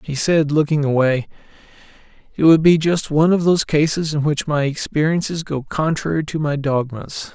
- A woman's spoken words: No, male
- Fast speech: No, average, 170 wpm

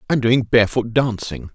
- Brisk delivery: No, average, 155 wpm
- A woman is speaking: No, male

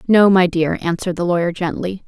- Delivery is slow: No, average, 200 wpm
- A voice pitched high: No, medium, 180 Hz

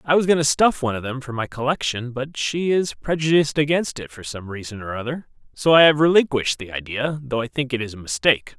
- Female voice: No, male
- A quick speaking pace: Yes, fast, 245 wpm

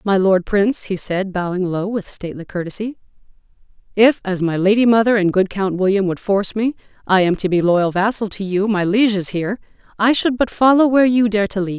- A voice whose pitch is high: Yes, high, 200 Hz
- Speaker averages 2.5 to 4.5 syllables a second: No, 5.7 syllables/s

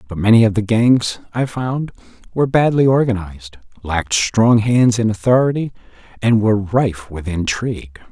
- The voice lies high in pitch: No, low, 110 Hz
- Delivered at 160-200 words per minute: No, average, 150 wpm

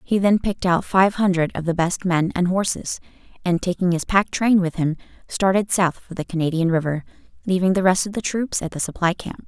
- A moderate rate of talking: No, fast, 220 wpm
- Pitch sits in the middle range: Yes, medium, 180 Hz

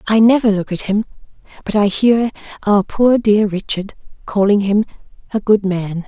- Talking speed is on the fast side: No, average, 170 wpm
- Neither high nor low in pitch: No, high, 205 Hz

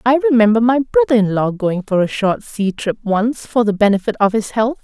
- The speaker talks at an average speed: No, fast, 235 wpm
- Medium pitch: No, high, 225 Hz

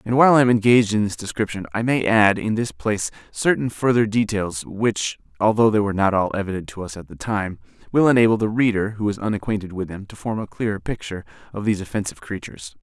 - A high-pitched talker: No, low, 105 Hz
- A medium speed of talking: No, fast, 220 wpm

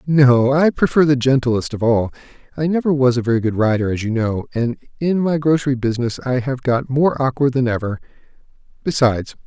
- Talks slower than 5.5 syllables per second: No, 5.6 syllables/s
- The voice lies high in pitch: No, low, 130 Hz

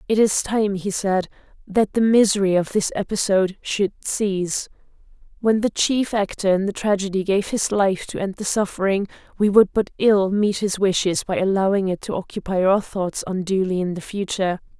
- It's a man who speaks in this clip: No, female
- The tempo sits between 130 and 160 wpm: No, average, 180 wpm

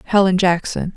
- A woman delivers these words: Yes, female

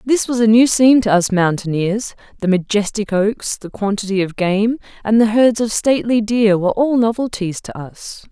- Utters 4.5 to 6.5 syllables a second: Yes, 5.0 syllables/s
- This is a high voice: Yes, high, 215 Hz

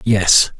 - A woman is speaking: No, male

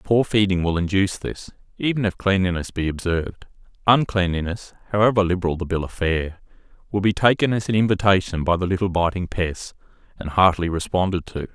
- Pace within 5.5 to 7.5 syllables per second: Yes, 5.9 syllables/s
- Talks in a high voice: No, very low, 95 Hz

